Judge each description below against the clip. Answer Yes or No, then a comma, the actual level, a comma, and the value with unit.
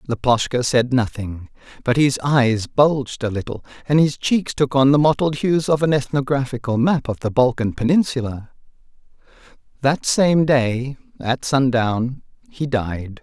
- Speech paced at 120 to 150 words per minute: Yes, average, 145 wpm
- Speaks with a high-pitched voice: No, low, 130 Hz